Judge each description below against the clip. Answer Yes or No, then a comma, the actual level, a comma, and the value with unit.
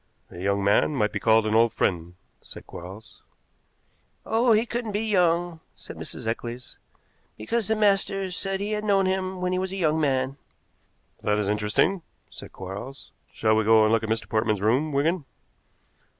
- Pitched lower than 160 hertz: Yes, medium, 140 Hz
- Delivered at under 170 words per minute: No, average, 180 wpm